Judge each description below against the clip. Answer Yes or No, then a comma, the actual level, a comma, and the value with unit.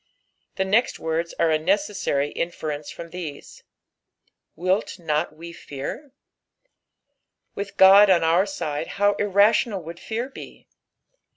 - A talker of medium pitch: Yes, medium, 175 Hz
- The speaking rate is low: Yes, slow, 125 wpm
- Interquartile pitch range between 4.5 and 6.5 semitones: No, average, 4.0 semitones